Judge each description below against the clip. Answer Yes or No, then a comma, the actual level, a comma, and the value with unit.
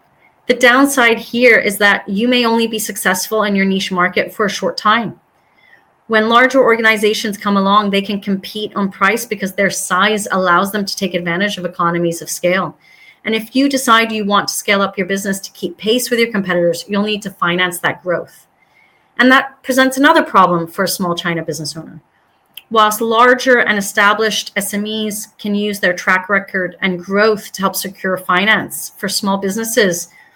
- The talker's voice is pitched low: No, high, 205 Hz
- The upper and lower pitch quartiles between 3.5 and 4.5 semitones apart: No, average, 2.7 semitones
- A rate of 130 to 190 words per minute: Yes, average, 185 wpm